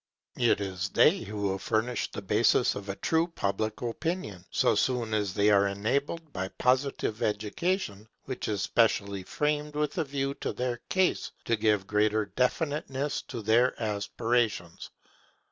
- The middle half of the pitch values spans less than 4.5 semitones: No, average, 5.3 semitones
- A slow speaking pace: No, average, 150 wpm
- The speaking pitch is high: No, low, 110 Hz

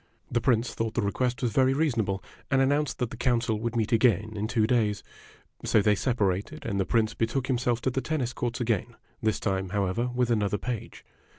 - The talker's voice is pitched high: No, low, 115 Hz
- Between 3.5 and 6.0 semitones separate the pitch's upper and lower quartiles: No, average, 2.8 semitones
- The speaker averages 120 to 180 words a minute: No, fast, 205 wpm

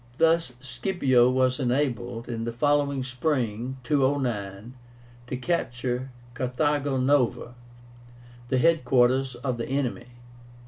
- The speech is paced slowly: Yes, slow, 105 wpm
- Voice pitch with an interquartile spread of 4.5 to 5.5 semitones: No, narrow, 2.5 semitones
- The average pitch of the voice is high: No, low, 130 Hz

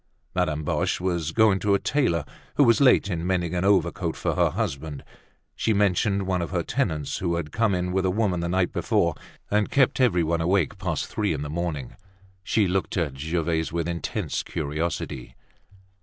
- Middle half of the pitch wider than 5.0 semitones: No, average, 3.3 semitones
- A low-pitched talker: Yes, very low, 90 Hz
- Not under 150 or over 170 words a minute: No, average, 185 wpm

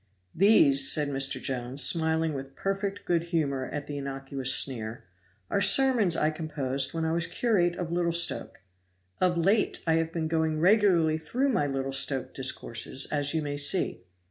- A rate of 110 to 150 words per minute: No, average, 170 wpm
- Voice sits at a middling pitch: Yes, medium, 160 Hz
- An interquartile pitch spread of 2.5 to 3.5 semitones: No, average, 4.3 semitones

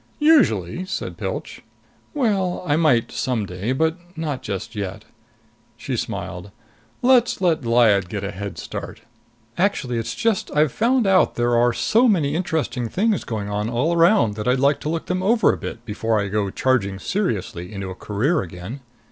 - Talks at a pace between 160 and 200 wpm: Yes, average, 175 wpm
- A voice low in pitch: Yes, low, 125 Hz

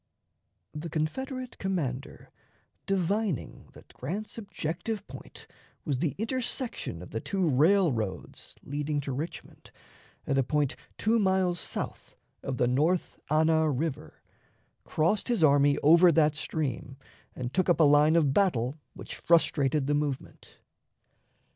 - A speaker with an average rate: No, slow, 130 wpm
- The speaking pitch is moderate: Yes, medium, 155 Hz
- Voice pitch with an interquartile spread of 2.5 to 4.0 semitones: No, average, 4.9 semitones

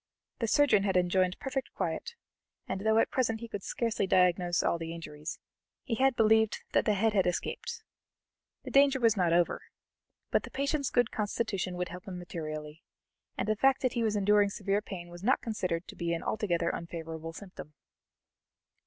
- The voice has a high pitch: Yes, high, 195 Hz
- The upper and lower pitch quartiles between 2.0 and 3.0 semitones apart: No, average, 4.5 semitones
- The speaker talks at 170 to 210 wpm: Yes, average, 180 wpm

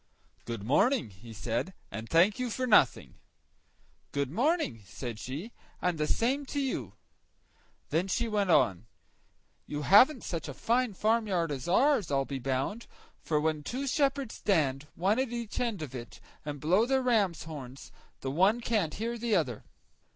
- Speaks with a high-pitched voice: No, medium, 180 Hz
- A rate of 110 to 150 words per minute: No, average, 165 wpm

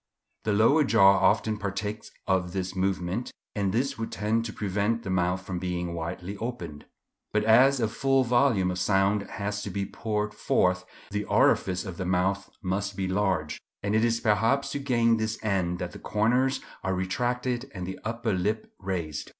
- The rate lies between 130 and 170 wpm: No, average, 180 wpm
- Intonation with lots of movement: No, average, 3.4 semitones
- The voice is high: No, low, 100 Hz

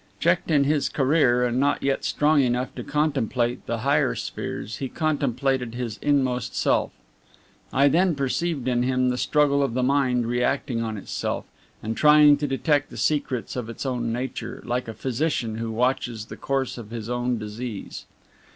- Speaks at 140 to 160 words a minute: No, average, 170 wpm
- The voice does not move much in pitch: No, average, 3.0 semitones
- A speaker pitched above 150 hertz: No, low, 130 Hz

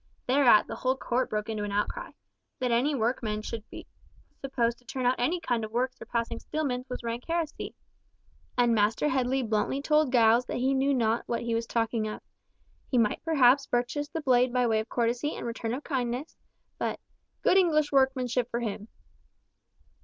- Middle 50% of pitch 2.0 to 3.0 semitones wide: Yes, average, 2.7 semitones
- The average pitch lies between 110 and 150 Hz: No, high, 245 Hz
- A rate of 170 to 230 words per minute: Yes, average, 180 wpm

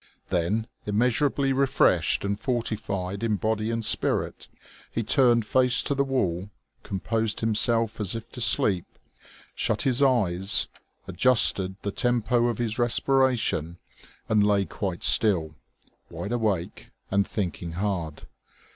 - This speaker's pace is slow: Yes, slow, 125 wpm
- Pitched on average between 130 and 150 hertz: No, low, 110 Hz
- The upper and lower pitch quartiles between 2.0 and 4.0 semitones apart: Yes, average, 3.6 semitones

